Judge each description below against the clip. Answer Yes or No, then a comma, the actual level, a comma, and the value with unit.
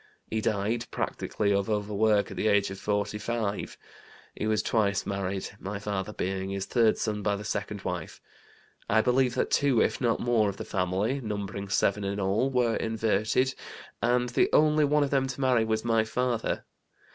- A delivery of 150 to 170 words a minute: No, average, 180 wpm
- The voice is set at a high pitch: No, low, 110 Hz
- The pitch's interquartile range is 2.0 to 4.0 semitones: Yes, average, 3.1 semitones